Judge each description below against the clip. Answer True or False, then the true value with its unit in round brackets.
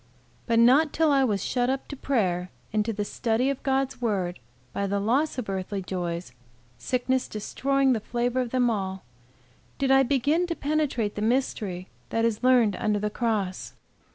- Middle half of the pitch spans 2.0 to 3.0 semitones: False (4.6 semitones)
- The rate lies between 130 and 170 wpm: False (180 wpm)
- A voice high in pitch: True (235 Hz)